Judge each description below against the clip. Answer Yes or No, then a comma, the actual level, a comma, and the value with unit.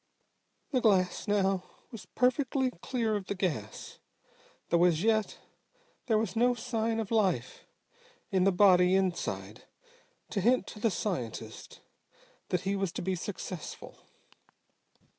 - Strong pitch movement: No, average, 3.7 semitones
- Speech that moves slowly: Yes, slow, 130 wpm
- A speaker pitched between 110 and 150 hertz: No, high, 200 Hz